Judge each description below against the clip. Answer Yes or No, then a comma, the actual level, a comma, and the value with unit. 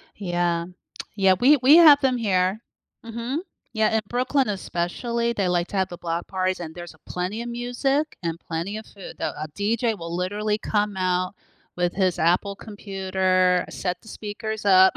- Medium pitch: No, high, 195 Hz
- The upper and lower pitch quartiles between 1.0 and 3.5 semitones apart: No, average, 4.1 semitones